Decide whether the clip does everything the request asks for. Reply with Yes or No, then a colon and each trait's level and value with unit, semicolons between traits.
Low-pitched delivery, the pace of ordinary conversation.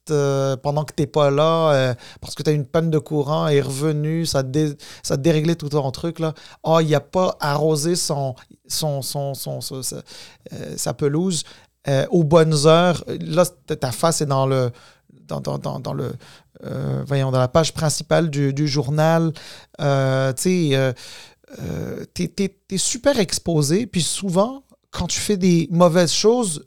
No: medium, 155 Hz; average, 175 wpm